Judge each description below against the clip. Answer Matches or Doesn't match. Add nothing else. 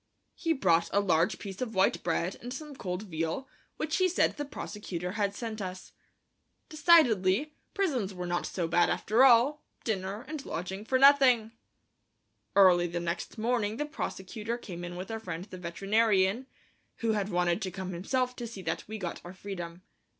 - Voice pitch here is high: Matches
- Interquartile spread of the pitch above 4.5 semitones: Matches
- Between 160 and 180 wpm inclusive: Matches